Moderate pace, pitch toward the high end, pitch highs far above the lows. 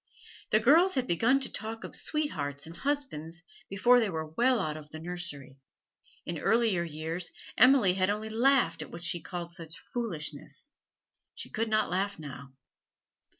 No: average, 160 wpm; medium, 180 Hz; wide, 6.6 semitones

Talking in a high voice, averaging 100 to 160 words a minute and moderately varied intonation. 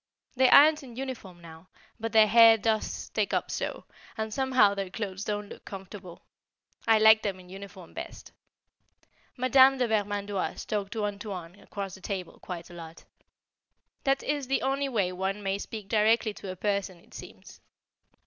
No: high, 205 Hz; average, 170 wpm; average, 3.0 semitones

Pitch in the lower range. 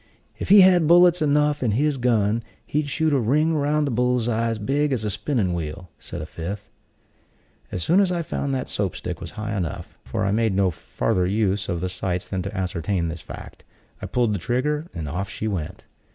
Yes: low, 110 Hz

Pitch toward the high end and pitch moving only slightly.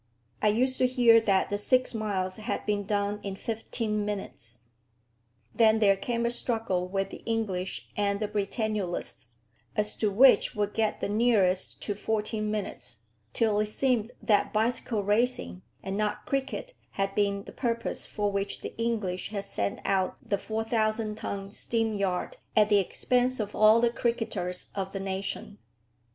Yes: high, 210 Hz; narrow, 2.3 semitones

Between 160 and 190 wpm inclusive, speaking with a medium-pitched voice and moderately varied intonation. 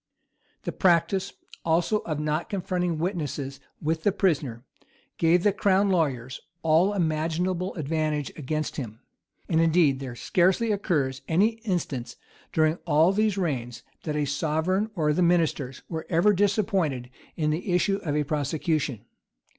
No: average, 140 wpm; medium, 160 Hz; average, 3.8 semitones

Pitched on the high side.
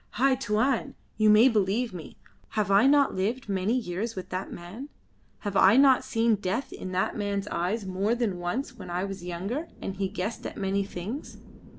Yes: high, 205 Hz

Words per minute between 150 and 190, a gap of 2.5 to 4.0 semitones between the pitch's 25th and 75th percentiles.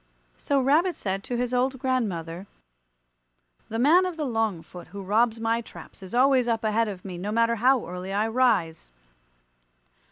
No: average, 170 wpm; average, 4.6 semitones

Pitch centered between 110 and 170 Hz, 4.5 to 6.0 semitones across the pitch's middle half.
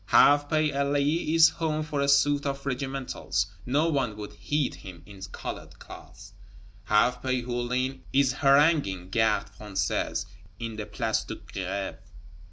Yes: low, 135 Hz; average, 5.2 semitones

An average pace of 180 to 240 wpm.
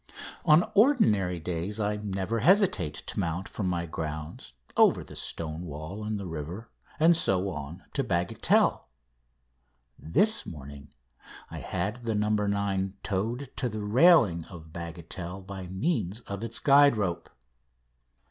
No: average, 140 wpm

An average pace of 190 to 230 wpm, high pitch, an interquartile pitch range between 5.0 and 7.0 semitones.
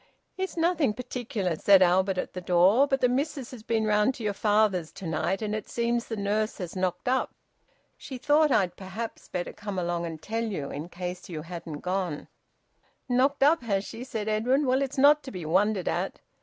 Yes: average, 200 wpm; high, 210 Hz; wide, 5.6 semitones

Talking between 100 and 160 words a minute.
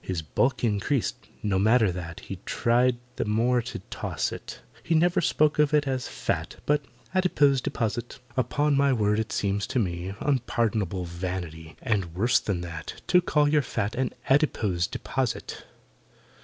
Yes: average, 155 wpm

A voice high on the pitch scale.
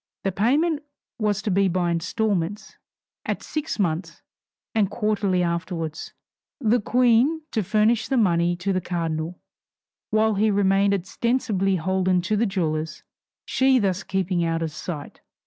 Yes: high, 195 Hz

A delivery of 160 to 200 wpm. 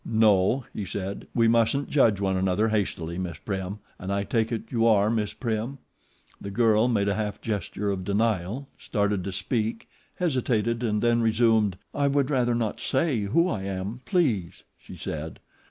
Yes: average, 170 wpm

